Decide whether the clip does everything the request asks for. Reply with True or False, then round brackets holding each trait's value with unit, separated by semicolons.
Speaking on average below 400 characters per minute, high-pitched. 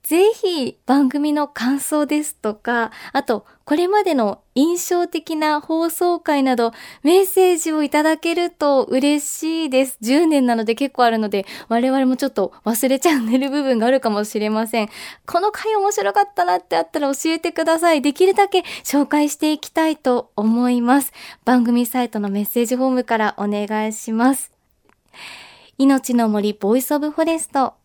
True (340 characters per minute; 275 Hz)